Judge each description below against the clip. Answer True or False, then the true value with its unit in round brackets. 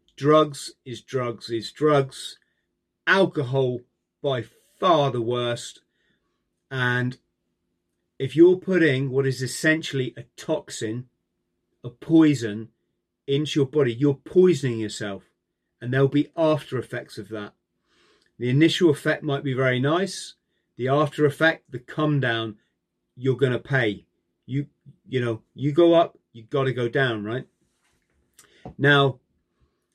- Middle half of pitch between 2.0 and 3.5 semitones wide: False (4.5 semitones)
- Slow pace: True (130 wpm)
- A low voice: True (130 Hz)